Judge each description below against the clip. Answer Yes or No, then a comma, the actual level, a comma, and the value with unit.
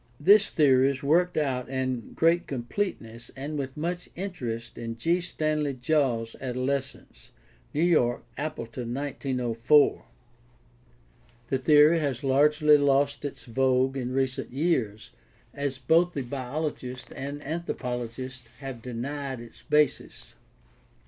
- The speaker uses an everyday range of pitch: Yes, average, 3.2 semitones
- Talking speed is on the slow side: Yes, slow, 115 wpm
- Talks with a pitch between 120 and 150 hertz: Yes, low, 135 Hz